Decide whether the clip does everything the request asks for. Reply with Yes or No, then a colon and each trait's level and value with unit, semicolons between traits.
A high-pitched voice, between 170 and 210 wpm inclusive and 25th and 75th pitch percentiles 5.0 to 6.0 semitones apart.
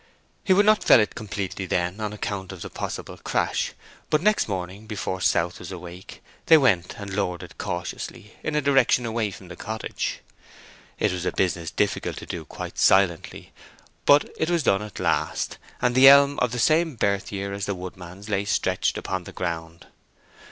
No: low, 100 Hz; average, 185 wpm; average, 5.3 semitones